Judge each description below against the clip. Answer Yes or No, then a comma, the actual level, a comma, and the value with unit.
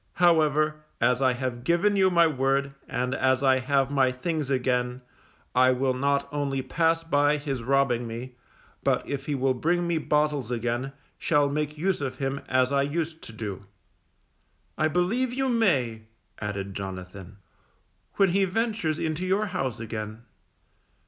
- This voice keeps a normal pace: Yes, average, 155 wpm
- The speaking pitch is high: No, medium, 140 Hz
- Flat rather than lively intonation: No, average, 4.4 semitones